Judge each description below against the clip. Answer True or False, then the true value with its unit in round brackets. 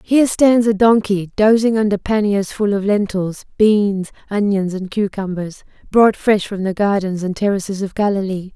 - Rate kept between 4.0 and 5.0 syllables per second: True (4.8 syllables/s)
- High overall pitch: True (200 Hz)